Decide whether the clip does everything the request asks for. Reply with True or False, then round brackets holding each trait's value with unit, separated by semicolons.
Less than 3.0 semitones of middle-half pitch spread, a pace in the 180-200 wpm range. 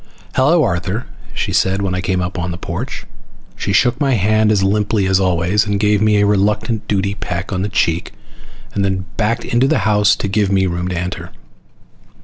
True (2.4 semitones; 195 wpm)